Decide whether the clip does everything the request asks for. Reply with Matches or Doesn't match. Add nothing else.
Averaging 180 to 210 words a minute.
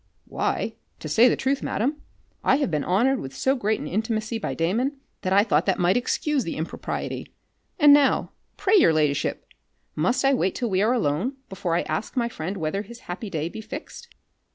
Matches